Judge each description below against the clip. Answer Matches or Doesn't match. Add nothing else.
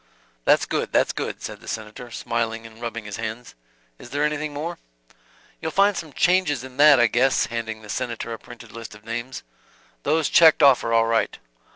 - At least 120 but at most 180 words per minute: Doesn't match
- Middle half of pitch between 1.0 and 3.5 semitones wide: Doesn't match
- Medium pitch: Doesn't match